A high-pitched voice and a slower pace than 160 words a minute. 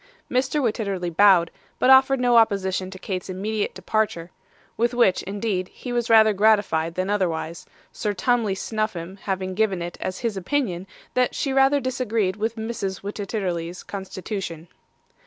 Yes: high, 200 Hz; average, 145 wpm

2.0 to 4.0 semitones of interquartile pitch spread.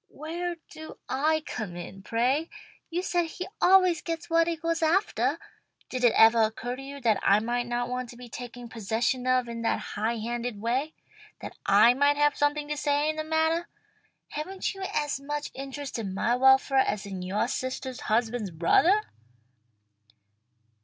No: average, 5.0 semitones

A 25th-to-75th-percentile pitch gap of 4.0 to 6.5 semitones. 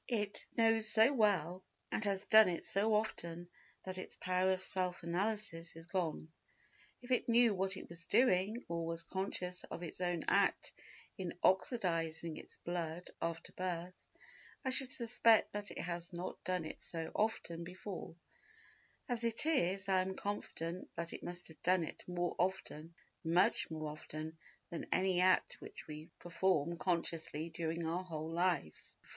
No: average, 3.0 semitones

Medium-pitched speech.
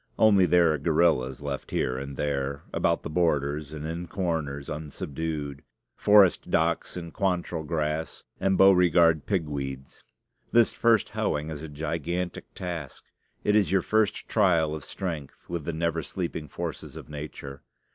No: very low, 80 Hz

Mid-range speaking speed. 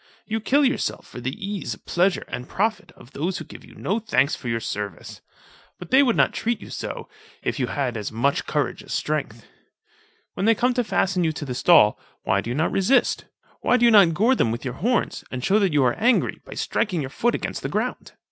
No: fast, 230 wpm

